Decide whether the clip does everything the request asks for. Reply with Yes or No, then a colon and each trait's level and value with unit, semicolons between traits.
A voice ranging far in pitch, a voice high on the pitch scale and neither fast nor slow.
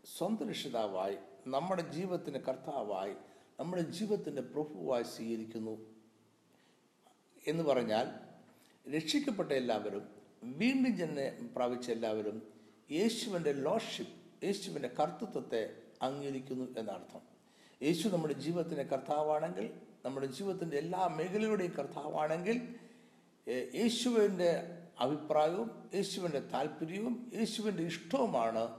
No: wide, 8.0 semitones; medium, 160 Hz; average, 80 wpm